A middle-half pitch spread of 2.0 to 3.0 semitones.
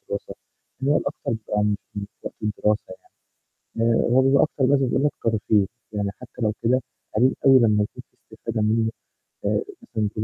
No: average, 3.4 semitones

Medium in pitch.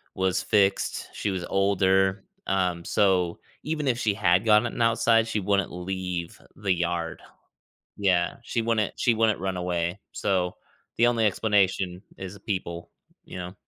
No: very low, 95 Hz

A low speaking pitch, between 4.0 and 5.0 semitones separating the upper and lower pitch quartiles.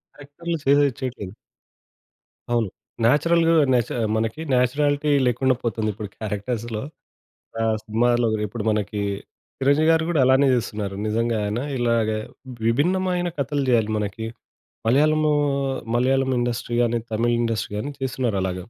Yes: low, 120 Hz; average, 4.4 semitones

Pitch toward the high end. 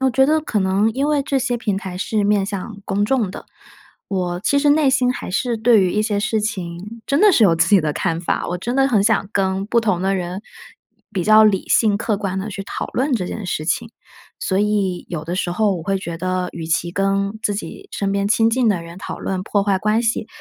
Yes: high, 200 Hz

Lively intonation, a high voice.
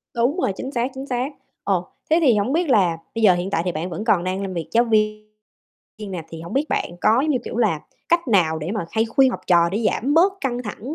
Yes: wide, 6.3 semitones; high, 215 Hz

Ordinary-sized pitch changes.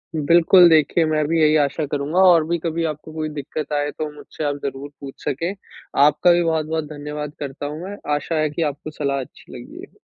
No: narrow, 2.0 semitones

